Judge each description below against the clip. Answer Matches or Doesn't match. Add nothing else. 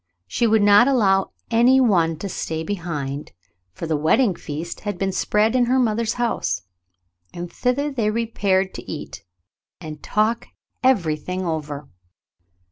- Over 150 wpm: Doesn't match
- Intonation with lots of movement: Matches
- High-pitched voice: Matches